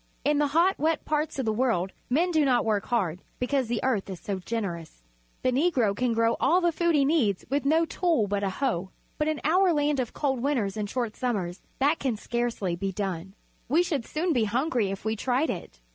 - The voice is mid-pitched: No, very high, 250 Hz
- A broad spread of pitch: Yes, wide, 6.6 semitones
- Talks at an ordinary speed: No, fast, 220 wpm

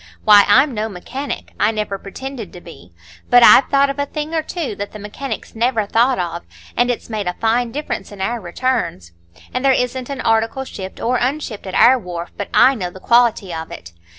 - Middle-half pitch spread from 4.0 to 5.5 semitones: Yes, average, 5.1 semitones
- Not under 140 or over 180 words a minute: No, fast, 205 wpm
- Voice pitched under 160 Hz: No, high, 225 Hz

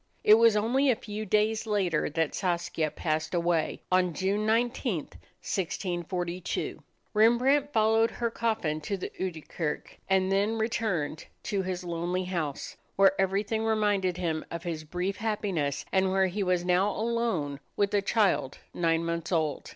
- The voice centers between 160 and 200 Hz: Yes, high, 190 Hz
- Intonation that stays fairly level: No, average, 4.1 semitones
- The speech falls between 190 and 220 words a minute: No, average, 150 wpm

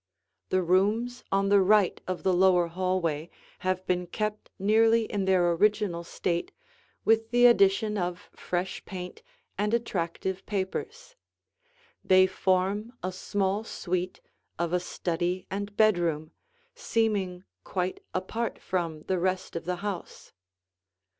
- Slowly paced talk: Yes, slow, 125 wpm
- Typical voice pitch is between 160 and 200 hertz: Yes, high, 190 Hz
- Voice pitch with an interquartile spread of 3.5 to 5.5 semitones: No, average, 2.8 semitones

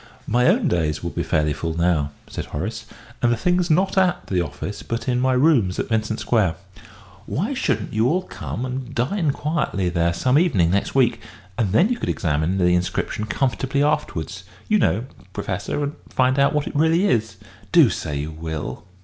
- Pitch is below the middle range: Yes, low, 115 Hz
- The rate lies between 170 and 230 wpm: Yes, average, 190 wpm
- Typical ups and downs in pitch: No, wide, 8.6 semitones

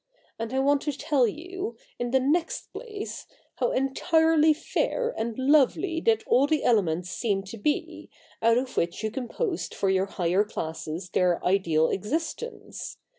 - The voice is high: Yes, very high, 255 Hz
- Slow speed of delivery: No, average, 155 wpm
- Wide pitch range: Yes, wide, 8.1 semitones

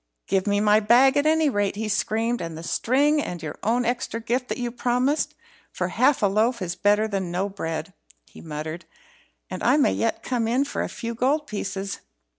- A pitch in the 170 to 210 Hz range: No, high, 225 Hz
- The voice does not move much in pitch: No, average, 4.3 semitones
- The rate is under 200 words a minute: No, fast, 205 wpm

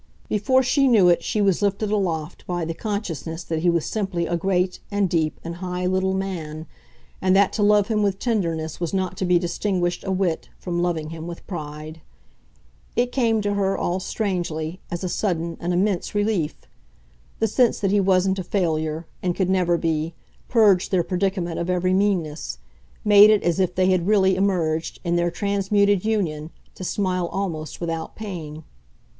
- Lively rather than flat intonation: No, average, 3.0 semitones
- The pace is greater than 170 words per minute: Yes, average, 180 wpm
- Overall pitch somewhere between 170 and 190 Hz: Yes, medium, 185 Hz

